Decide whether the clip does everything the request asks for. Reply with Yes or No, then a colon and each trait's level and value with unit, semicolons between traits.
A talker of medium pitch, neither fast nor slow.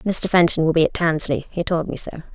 No: medium, 165 Hz; fast, 255 wpm